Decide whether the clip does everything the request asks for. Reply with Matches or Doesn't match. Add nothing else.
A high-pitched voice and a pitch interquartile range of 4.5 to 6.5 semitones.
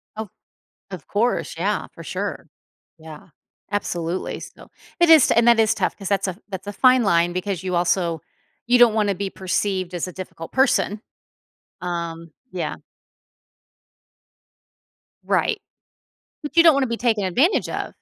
Matches